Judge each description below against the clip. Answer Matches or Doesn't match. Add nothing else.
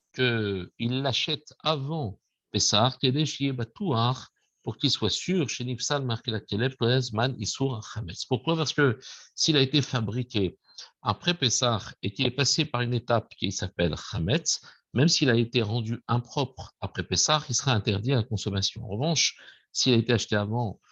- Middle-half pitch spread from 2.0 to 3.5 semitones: Doesn't match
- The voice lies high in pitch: Doesn't match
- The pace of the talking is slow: Matches